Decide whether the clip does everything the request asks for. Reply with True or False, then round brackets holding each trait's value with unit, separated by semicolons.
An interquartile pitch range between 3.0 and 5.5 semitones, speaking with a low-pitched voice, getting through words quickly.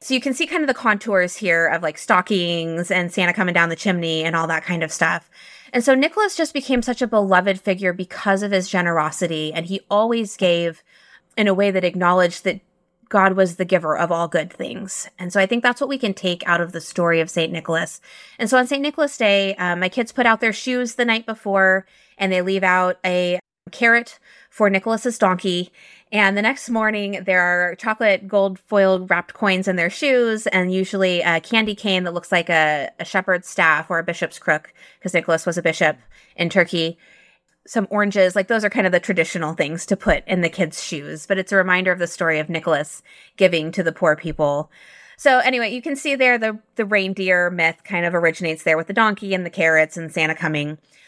False (4.1 semitones; 185 Hz; 220 wpm)